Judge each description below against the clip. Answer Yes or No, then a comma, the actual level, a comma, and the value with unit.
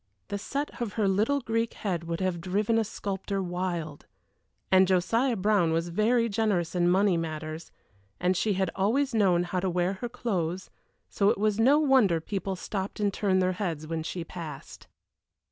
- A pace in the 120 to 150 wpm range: No, average, 180 wpm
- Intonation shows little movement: No, average, 3.7 semitones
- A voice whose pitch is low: No, high, 190 Hz